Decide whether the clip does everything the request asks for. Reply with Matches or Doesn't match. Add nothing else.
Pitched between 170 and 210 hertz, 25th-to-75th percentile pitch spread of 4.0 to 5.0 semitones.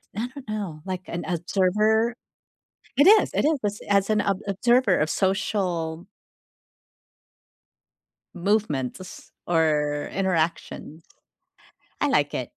Matches